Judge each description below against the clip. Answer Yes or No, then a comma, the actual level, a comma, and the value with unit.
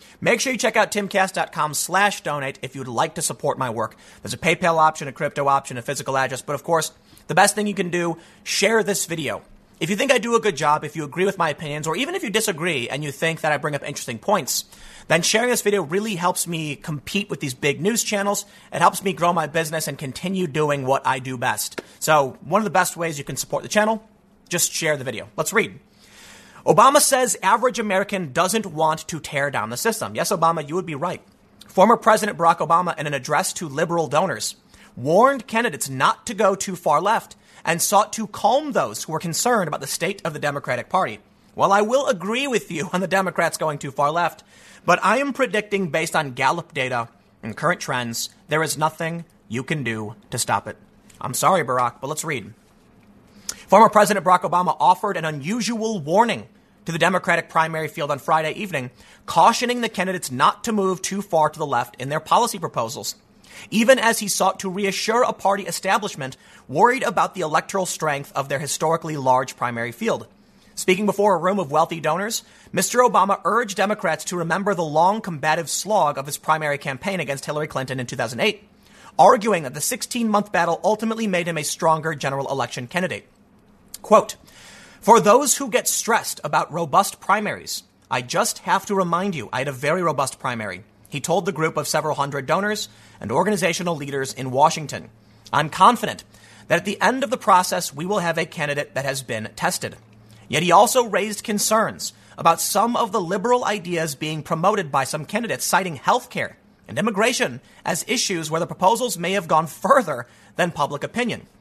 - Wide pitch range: Yes, wide, 5.7 semitones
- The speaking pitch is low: No, medium, 170 Hz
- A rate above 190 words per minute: Yes, average, 200 wpm